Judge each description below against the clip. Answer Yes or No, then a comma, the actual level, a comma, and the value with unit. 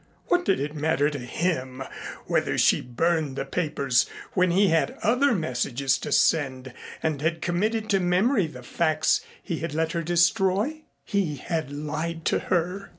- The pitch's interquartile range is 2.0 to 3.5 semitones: No, average, 4.3 semitones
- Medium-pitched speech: Yes, medium, 165 Hz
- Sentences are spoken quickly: No, average, 160 wpm